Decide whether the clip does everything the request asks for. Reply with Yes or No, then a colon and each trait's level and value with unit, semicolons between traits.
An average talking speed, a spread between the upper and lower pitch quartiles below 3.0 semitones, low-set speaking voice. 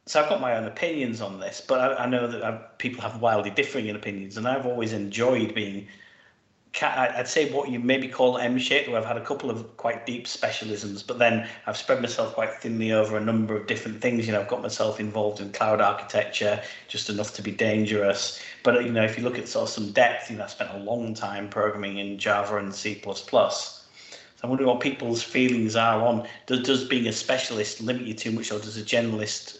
No: fast, 225 wpm; narrow, 2.5 semitones; low, 110 Hz